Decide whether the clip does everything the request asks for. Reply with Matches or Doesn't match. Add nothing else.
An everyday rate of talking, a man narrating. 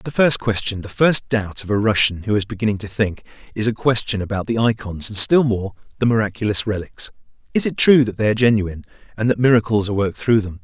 Doesn't match